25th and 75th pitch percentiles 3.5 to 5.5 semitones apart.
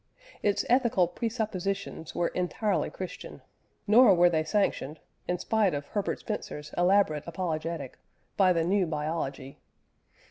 Yes: average, 4.3 semitones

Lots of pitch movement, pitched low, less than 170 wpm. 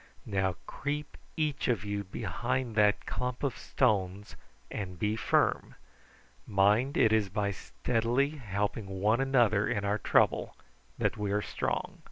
No: average, 3.7 semitones; low, 105 Hz; average, 140 wpm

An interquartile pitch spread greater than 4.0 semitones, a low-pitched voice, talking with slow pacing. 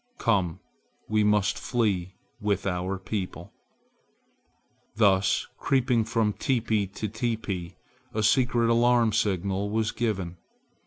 No: average, 3.1 semitones; low, 105 Hz; slow, 105 wpm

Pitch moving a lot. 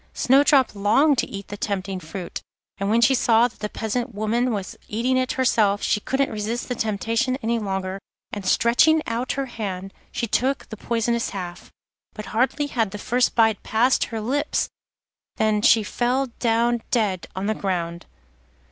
No: average, 3.3 semitones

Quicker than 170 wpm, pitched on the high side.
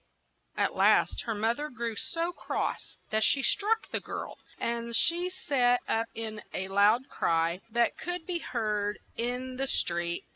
No: average, 160 wpm; high, 235 Hz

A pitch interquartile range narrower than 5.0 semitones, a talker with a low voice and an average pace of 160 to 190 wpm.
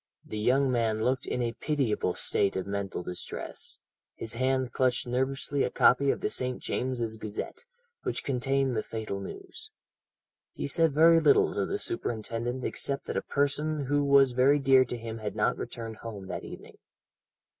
Yes: average, 3.6 semitones; low, 130 Hz; average, 170 wpm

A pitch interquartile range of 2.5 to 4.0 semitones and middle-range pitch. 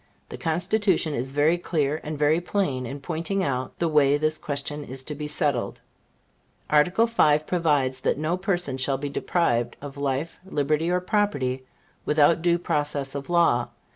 Yes: average, 3.7 semitones; medium, 150 Hz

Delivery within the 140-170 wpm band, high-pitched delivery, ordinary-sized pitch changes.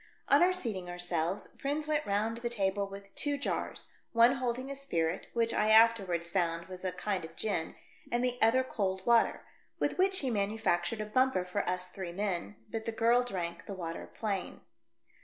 No: average, 190 wpm; high, 210 Hz; average, 4.7 semitones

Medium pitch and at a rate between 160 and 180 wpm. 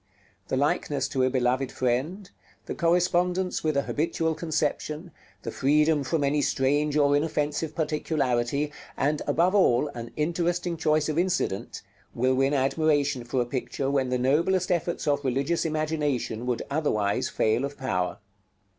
No: medium, 145 Hz; average, 145 wpm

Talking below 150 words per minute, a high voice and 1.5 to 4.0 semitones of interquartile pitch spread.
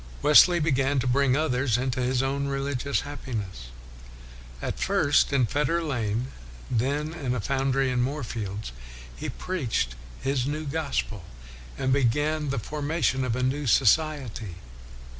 No: average, 140 wpm; low, 135 Hz; average, 3.1 semitones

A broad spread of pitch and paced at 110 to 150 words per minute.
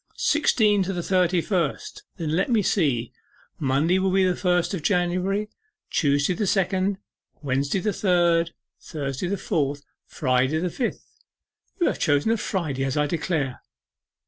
No: average, 4.8 semitones; average, 140 wpm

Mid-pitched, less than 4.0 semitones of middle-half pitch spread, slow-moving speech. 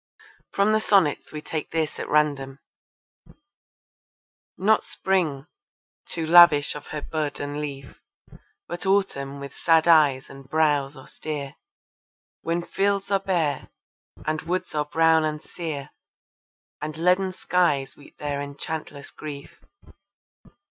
Yes: medium, 155 Hz; average, 3.3 semitones; slow, 120 wpm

